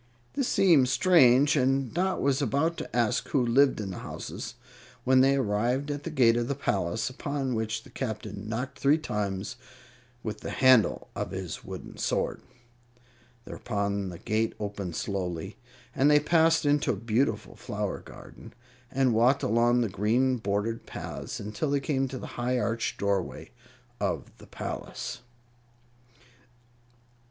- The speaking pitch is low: Yes, low, 125 Hz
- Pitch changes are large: No, average, 4.6 semitones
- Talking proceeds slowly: No, average, 145 wpm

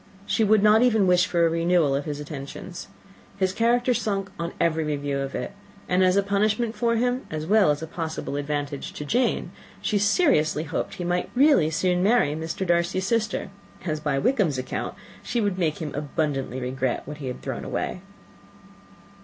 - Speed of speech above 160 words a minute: Yes, average, 185 wpm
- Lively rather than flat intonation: Yes, wide, 5.7 semitones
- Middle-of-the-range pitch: Yes, medium, 175 Hz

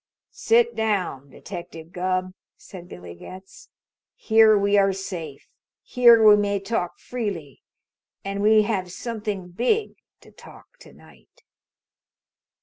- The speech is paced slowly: Yes, slow, 120 wpm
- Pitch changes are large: No, average, 3.6 semitones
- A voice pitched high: Yes, high, 200 Hz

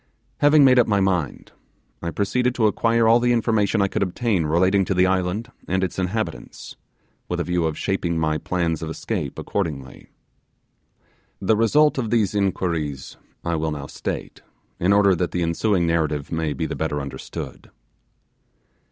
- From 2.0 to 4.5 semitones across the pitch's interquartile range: No, average, 5.0 semitones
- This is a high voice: No, very low, 95 Hz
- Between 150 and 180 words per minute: Yes, average, 165 wpm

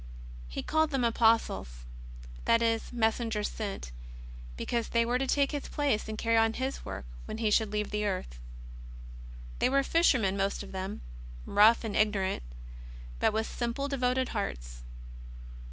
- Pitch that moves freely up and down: No, average, 3.4 semitones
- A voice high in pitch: Yes, high, 225 Hz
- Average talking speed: Yes, average, 155 wpm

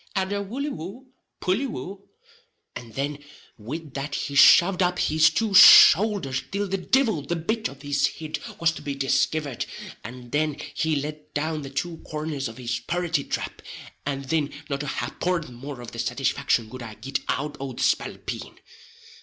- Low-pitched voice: No, medium, 150 Hz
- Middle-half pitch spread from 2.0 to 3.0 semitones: No, average, 4.7 semitones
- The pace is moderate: Yes, average, 175 wpm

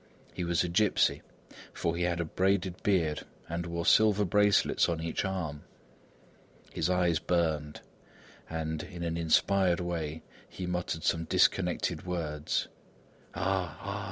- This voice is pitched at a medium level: No, very low, 85 Hz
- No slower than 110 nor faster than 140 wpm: Yes, slow, 135 wpm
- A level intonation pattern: Yes, narrow, 2.3 semitones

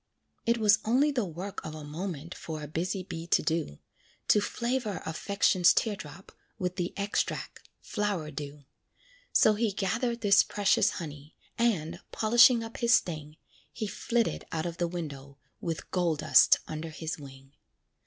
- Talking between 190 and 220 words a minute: No, average, 155 wpm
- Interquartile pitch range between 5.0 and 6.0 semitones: Yes, average, 5.3 semitones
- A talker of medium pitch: Yes, medium, 180 Hz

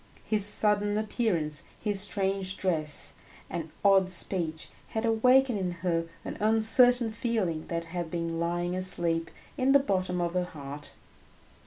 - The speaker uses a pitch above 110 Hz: Yes, medium, 185 Hz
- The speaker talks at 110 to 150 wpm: Yes, average, 140 wpm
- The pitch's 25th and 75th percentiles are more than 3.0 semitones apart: Yes, average, 4.4 semitones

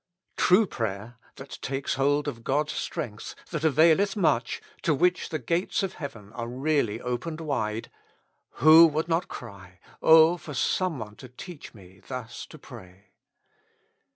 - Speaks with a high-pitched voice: No, medium, 140 Hz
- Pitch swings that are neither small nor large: No, wide, 5.8 semitones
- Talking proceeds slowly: No, average, 155 wpm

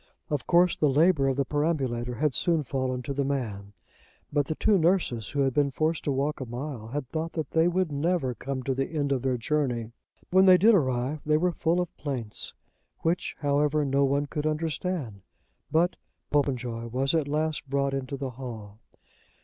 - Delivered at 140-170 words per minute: No, average, 190 wpm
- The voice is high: No, medium, 140 Hz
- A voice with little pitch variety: No, average, 3.4 semitones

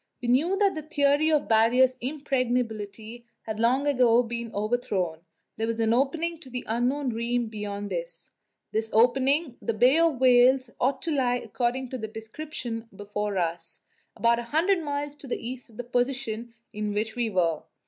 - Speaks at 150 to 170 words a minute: No, average, 180 wpm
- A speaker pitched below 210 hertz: No, high, 245 Hz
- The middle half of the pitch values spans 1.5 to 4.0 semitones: Yes, average, 3.6 semitones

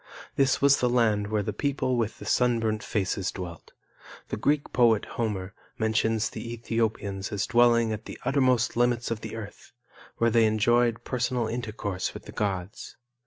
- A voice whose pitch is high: No, low, 115 Hz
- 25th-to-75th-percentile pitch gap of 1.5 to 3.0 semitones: Yes, narrow, 2.6 semitones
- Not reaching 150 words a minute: No, average, 165 wpm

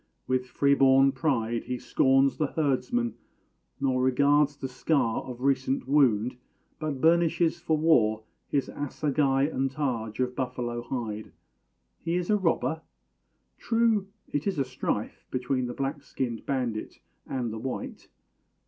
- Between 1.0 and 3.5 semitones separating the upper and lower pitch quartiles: Yes, average, 2.8 semitones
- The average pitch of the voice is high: No, low, 135 Hz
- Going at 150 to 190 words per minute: No, slow, 135 wpm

